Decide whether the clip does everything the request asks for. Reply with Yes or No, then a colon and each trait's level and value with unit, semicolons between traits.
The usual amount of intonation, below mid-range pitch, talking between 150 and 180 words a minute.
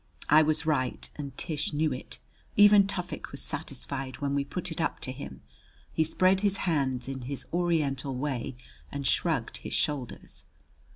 No: average, 3.9 semitones; medium, 145 Hz; average, 165 wpm